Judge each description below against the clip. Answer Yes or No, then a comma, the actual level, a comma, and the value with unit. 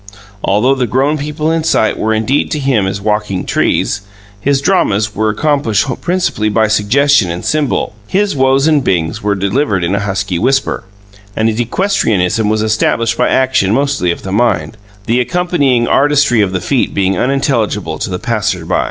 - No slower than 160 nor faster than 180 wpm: Yes, average, 170 wpm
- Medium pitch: No, low, 115 Hz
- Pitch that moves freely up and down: Yes, wide, 5.8 semitones